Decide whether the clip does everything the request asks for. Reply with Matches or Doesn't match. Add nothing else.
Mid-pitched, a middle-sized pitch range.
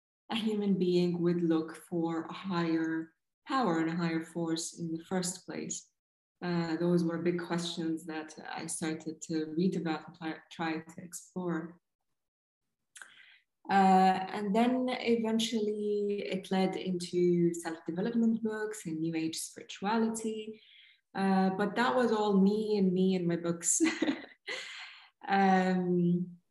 Matches